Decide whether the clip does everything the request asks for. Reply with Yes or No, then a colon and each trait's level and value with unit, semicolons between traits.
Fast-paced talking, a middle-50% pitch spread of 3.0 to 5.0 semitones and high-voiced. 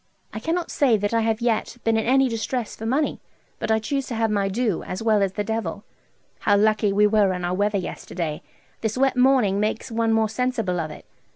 No: fast, 220 wpm; narrow, 2.6 semitones; high, 220 Hz